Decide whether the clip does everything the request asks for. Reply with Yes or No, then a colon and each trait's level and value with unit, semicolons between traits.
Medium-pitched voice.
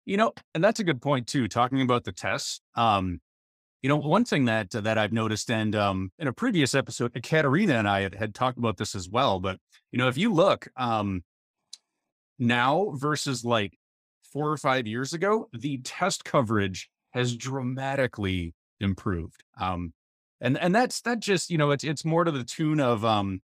No: low, 120 Hz